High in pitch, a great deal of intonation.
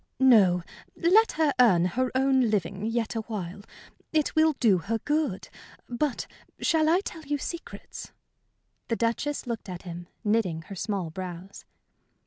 Yes: high, 230 Hz; wide, 7.4 semitones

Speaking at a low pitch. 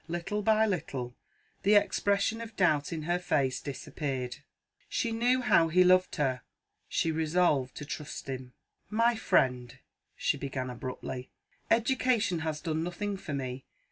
No: medium, 165 Hz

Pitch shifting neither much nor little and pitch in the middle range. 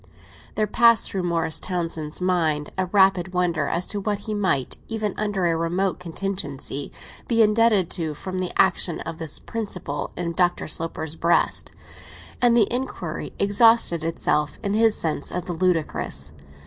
Yes: average, 3.7 semitones; medium, 180 Hz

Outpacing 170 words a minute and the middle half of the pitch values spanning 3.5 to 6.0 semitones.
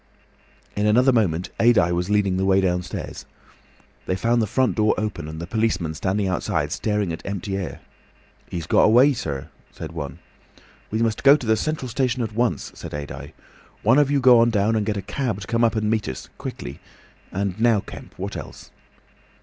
Yes: average, 190 wpm; average, 4.2 semitones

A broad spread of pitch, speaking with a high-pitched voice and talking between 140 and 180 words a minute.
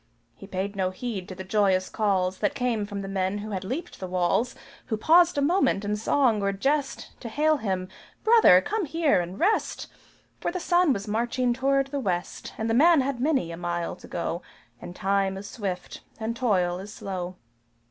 No: wide, 6.4 semitones; high, 210 Hz; average, 195 wpm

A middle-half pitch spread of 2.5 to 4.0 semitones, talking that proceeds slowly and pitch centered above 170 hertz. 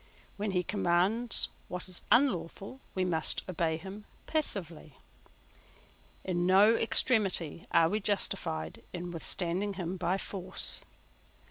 Yes: average, 3.1 semitones; slow, 115 wpm; medium, 185 Hz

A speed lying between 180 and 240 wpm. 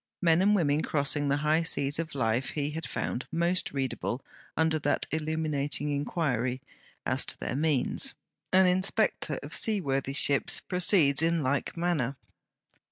No: average, 150 wpm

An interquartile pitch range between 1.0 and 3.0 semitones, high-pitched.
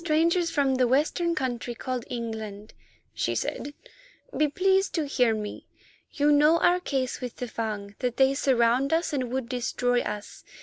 No: average, 4.4 semitones; very high, 260 Hz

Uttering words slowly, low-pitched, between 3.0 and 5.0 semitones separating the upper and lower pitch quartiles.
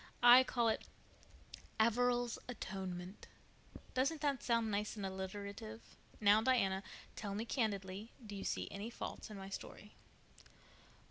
No: slow, 130 wpm; high, 210 Hz; average, 3.6 semitones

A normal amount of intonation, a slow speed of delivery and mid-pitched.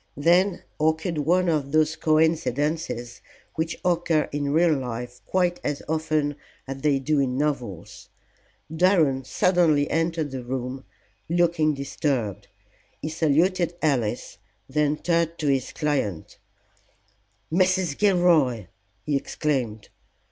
Yes: average, 3.6 semitones; slow, 110 wpm; medium, 150 Hz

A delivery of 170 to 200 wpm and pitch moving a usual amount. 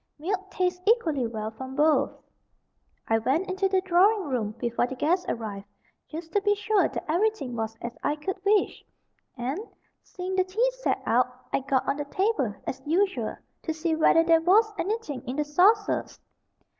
No: average, 175 wpm; wide, 6.9 semitones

